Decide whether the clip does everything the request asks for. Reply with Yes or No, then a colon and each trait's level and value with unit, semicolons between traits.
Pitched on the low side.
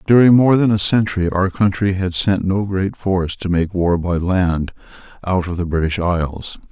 Yes: very low, 95 Hz